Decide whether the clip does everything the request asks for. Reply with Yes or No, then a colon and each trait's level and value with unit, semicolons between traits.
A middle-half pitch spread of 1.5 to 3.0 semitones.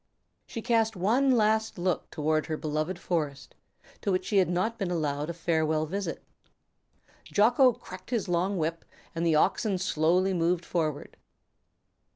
No: average, 4.5 semitones